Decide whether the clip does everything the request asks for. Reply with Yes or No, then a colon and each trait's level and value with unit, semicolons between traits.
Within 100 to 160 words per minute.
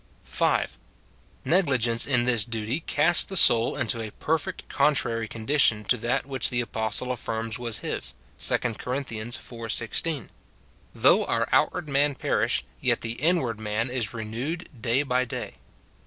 Yes: average, 155 wpm